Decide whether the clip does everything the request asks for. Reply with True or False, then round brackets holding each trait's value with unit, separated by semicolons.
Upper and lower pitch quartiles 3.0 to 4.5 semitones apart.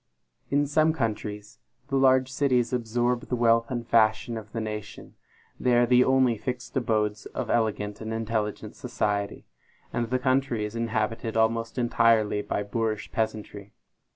False (2.6 semitones)